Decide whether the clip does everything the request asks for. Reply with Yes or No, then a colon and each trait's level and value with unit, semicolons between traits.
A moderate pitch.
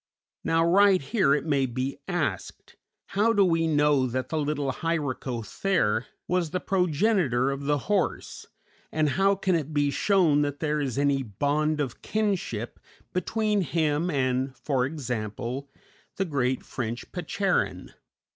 Yes: medium, 150 Hz